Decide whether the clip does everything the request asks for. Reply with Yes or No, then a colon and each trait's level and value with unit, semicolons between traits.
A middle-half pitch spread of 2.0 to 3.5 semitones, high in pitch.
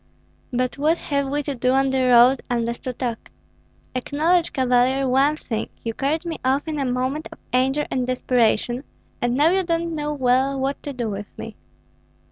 Yes: average, 2.8 semitones; very high, 265 Hz